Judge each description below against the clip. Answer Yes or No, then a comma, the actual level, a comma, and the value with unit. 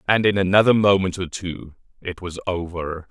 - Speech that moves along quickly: No, average, 175 wpm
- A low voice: Yes, very low, 90 Hz